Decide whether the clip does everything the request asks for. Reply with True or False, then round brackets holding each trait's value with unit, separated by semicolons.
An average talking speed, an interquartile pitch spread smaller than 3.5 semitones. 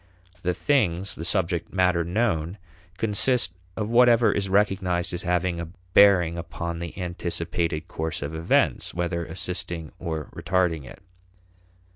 False (130 wpm; 2.5 semitones)